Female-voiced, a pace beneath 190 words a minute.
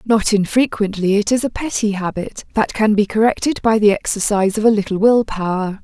No: female; average, 195 wpm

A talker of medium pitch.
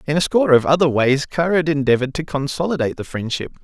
Yes: medium, 145 Hz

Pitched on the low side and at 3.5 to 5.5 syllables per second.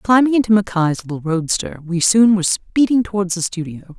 No: high, 190 Hz; 5.4 syllables/s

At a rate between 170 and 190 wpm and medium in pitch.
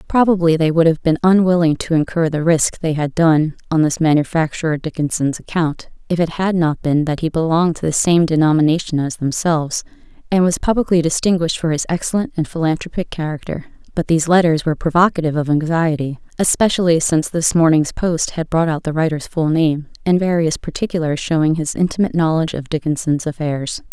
Yes: average, 180 wpm; medium, 160 Hz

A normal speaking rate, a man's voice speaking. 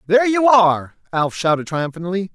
Yes: average, 155 wpm; male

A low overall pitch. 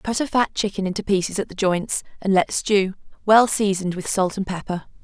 No: high, 195 Hz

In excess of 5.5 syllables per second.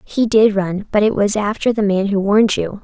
No: 5.2 syllables/s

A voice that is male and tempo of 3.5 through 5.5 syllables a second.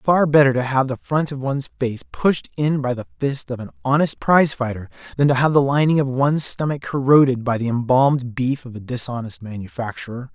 No: male; 5.7 syllables/s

